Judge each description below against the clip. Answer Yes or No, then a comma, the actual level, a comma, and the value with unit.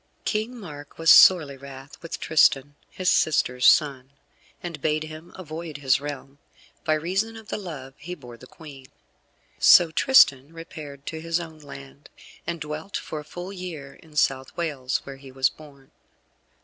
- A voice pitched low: No, medium, 150 Hz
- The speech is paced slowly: No, average, 160 wpm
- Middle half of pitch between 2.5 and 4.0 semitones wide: Yes, average, 3.5 semitones